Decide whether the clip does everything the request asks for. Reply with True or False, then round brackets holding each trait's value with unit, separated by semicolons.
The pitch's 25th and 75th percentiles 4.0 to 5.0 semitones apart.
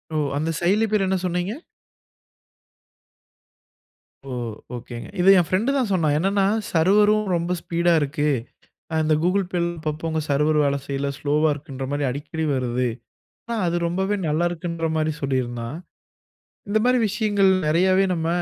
True (4.5 semitones)